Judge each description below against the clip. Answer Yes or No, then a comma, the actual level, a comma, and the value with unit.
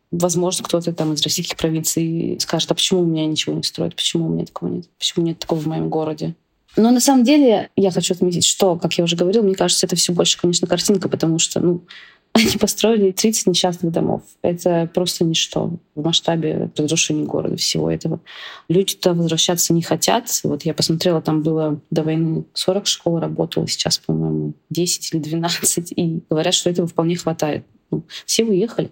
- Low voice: No, medium, 170 Hz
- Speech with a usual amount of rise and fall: No, narrow, 2.2 semitones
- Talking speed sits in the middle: No, fast, 185 wpm